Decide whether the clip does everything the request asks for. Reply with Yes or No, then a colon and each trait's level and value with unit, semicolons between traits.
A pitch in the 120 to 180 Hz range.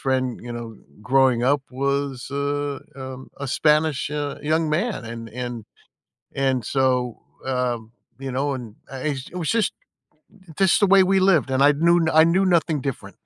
Yes: low, 135 Hz